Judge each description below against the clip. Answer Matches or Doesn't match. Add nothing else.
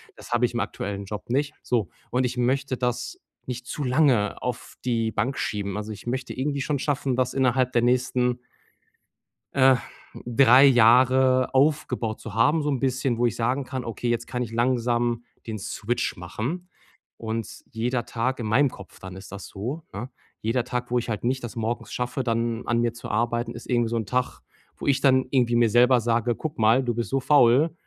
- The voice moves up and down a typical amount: Doesn't match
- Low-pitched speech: Matches